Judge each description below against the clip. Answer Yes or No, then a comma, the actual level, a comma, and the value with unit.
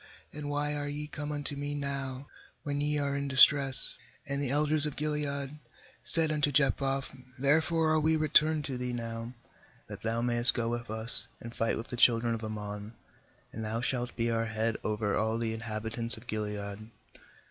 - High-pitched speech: No, low, 130 Hz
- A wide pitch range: No, average, 4.2 semitones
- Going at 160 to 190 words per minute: Yes, average, 180 wpm